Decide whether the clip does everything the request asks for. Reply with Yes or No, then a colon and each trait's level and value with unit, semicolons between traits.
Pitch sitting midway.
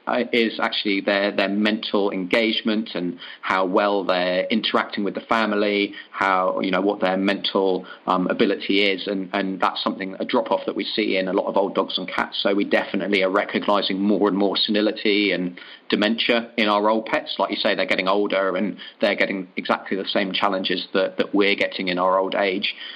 No: low, 100 Hz